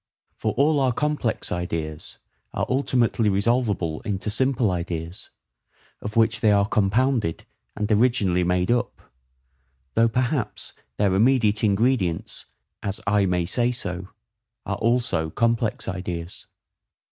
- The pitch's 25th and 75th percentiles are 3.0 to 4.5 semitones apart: No, average, 5.1 semitones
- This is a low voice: Yes, low, 105 Hz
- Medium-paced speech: No, slow, 120 wpm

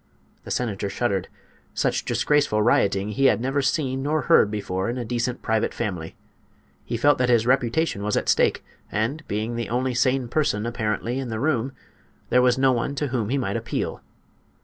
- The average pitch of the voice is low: Yes, low, 120 Hz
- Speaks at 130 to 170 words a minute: No, average, 185 wpm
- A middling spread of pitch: Yes, average, 3.7 semitones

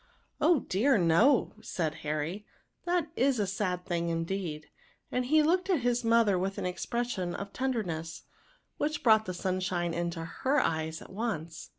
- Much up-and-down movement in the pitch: Yes, wide, 6.4 semitones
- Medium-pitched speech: No, high, 195 Hz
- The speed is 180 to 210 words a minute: Yes, average, 185 wpm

